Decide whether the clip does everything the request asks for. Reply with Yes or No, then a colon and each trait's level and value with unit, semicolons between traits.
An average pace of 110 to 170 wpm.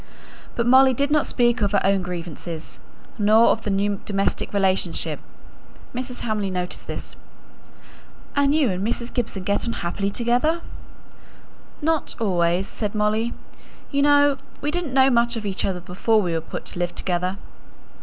Yes: average, 160 wpm